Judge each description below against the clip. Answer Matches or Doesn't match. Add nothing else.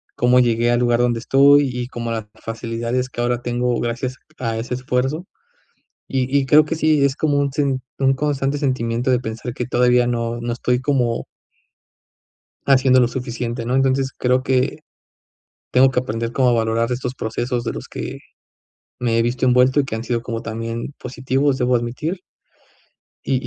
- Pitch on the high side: Doesn't match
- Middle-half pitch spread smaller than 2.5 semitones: Matches